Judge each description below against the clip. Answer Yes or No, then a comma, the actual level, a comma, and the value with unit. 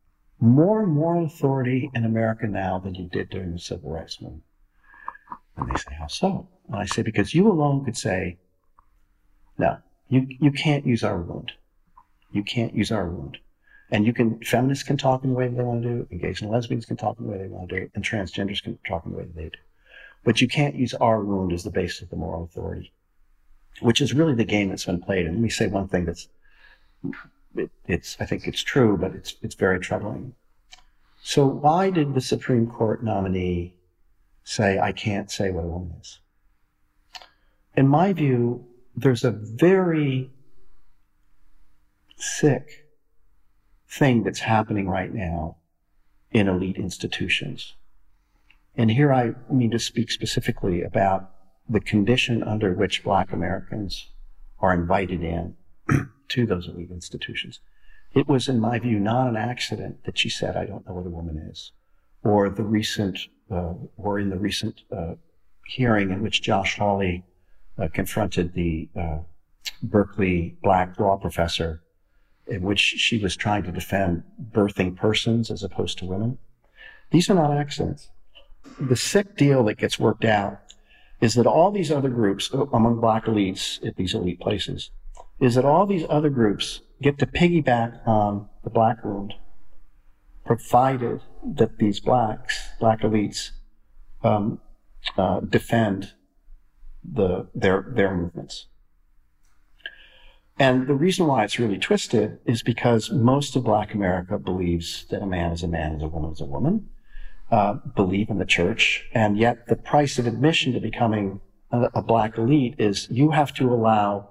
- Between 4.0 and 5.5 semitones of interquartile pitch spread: Yes, average, 4.8 semitones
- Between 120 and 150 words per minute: No, average, 165 wpm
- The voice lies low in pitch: Yes, low, 105 Hz